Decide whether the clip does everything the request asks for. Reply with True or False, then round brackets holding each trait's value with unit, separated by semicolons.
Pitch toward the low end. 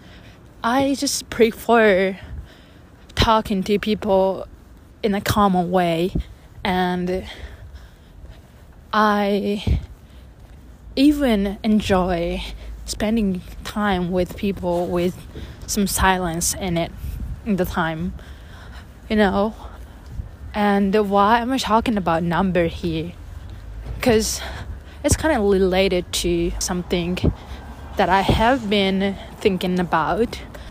False (190 Hz)